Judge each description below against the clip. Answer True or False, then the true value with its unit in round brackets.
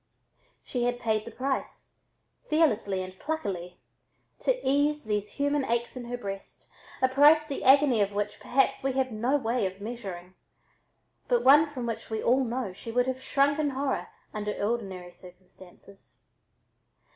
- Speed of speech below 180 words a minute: True (155 wpm)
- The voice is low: False (245 Hz)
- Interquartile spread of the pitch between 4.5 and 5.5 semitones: True (5.2 semitones)